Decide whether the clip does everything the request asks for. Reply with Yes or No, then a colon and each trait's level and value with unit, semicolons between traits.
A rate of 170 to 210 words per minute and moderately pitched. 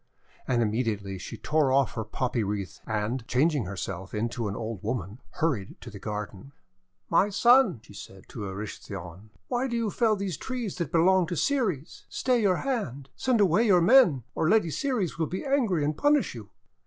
Yes: average, 185 wpm; medium, 145 Hz